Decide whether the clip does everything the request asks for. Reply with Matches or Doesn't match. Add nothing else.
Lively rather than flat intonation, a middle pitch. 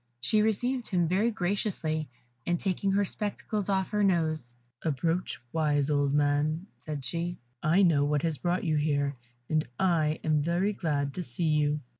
Doesn't match